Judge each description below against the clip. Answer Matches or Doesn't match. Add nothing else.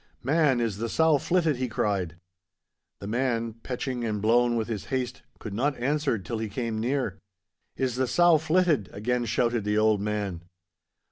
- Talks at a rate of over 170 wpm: Doesn't match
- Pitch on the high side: Doesn't match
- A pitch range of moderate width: Matches